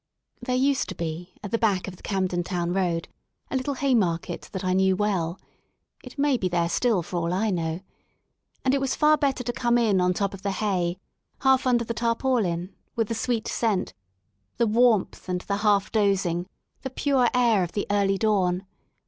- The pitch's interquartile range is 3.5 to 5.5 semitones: Yes, average, 4.9 semitones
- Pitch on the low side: No, high, 200 Hz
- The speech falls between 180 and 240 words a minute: Yes, average, 200 wpm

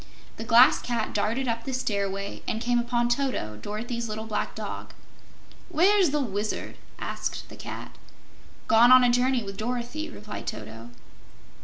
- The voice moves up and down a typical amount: Yes, average, 3.0 semitones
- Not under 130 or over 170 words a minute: Yes, average, 150 wpm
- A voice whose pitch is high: Yes, high, 235 Hz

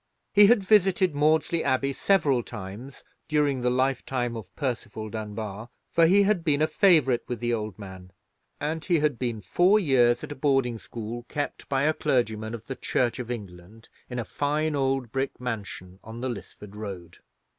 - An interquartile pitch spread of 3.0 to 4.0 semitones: No, average, 5.2 semitones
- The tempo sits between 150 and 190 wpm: Yes, average, 175 wpm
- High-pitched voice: No, low, 125 Hz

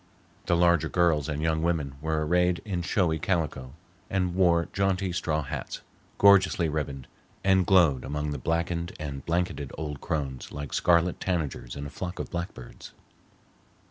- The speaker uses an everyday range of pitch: Yes, average, 3.3 semitones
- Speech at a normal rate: Yes, average, 150 wpm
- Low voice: Yes, very low, 85 Hz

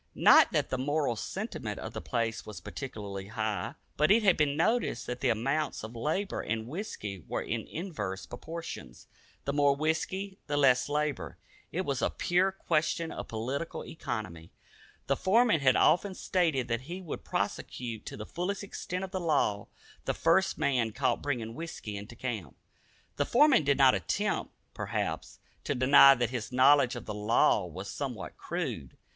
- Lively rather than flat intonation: Yes, wide, 6.7 semitones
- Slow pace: No, average, 170 wpm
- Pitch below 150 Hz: Yes, medium, 140 Hz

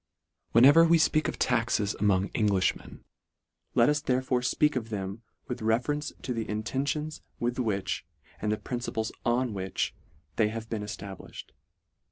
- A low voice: Yes, low, 115 Hz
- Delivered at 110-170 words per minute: Yes, average, 145 wpm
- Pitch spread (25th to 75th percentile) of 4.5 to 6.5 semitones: No, average, 3.6 semitones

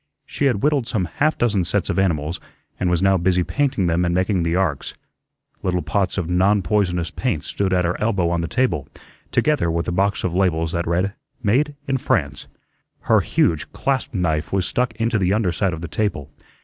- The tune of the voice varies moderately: Yes, average, 3.9 semitones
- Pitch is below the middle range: Yes, very low, 95 Hz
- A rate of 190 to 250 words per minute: Yes, average, 200 wpm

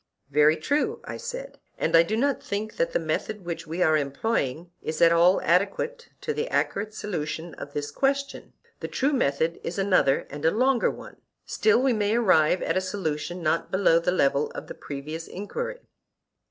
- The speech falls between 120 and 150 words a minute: No, average, 185 wpm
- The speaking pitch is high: No, medium, 180 Hz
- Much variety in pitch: Yes, wide, 6.8 semitones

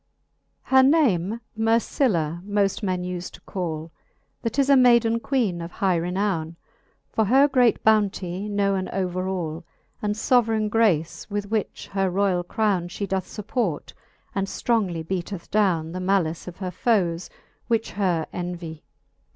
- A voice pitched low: No, high, 195 Hz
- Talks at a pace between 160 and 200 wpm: No, average, 150 wpm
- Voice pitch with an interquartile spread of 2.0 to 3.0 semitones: No, average, 3.9 semitones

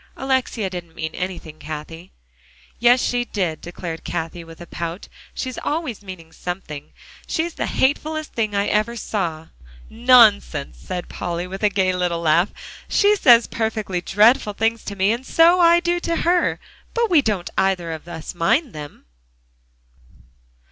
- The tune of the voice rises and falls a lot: Yes, wide, 6.3 semitones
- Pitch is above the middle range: Yes, high, 200 Hz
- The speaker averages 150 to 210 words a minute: Yes, average, 155 wpm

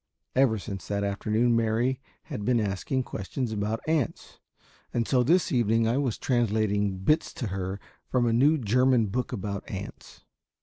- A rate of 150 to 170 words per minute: Yes, average, 160 wpm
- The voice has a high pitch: No, low, 115 Hz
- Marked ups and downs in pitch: No, average, 3.7 semitones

